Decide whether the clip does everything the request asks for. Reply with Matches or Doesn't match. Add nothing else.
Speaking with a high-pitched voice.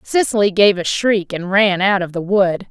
Matches